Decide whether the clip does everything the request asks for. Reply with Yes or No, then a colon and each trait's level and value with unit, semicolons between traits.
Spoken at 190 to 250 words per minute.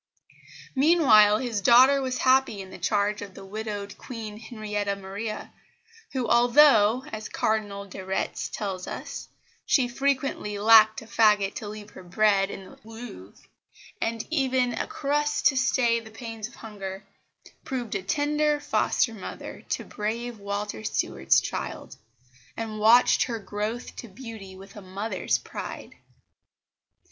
No: average, 140 wpm